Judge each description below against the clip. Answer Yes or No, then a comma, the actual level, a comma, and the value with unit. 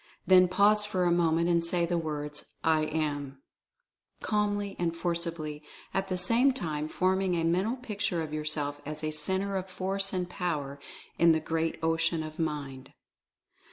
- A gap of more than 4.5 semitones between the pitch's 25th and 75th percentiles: No, average, 3.5 semitones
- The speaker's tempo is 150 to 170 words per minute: Yes, average, 160 wpm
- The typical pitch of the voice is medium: Yes, medium, 170 Hz